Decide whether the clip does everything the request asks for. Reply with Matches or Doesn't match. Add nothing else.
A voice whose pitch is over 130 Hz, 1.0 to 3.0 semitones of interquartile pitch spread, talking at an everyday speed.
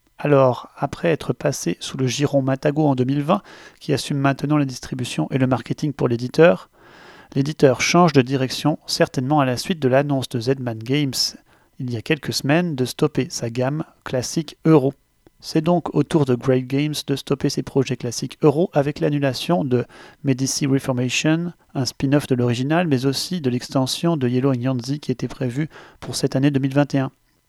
Matches